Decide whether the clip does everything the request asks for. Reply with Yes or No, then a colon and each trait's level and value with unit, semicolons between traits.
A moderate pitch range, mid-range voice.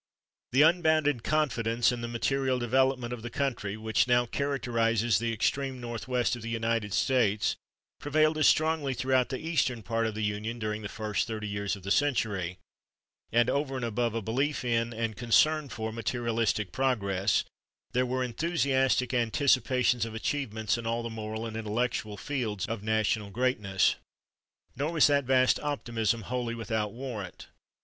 No: average, 3.1 semitones; low, 120 Hz